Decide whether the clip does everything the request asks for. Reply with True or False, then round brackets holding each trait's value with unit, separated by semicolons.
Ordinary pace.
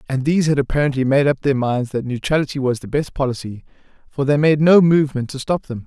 False (225 wpm)